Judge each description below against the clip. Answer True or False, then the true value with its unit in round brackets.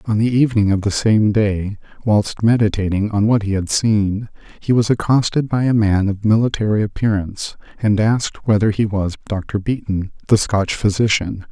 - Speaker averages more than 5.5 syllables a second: False (5.0 syllables/s)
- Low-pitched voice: True (105 Hz)